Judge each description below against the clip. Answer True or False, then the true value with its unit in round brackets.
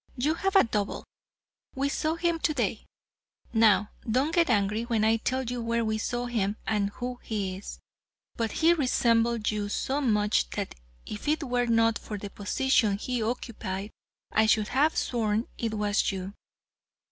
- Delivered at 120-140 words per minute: False (165 wpm)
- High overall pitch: True (230 Hz)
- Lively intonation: False (3.5 semitones)